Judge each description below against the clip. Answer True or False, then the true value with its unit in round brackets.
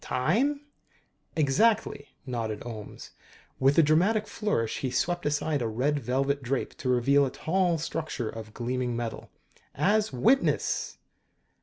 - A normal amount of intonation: False (6.0 semitones)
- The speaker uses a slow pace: True (130 wpm)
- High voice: False (140 Hz)